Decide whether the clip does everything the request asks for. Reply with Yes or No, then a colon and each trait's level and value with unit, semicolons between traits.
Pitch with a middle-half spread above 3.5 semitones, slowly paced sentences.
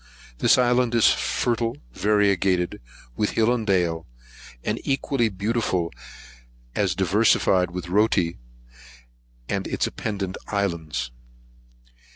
Yes: average, 4.3 semitones; slow, 100 wpm